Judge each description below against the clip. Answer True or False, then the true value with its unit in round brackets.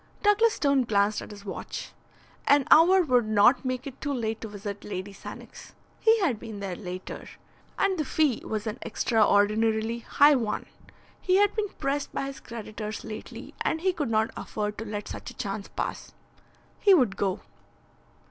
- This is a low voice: False (230 Hz)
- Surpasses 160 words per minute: True (175 wpm)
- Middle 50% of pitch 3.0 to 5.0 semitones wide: False (5.6 semitones)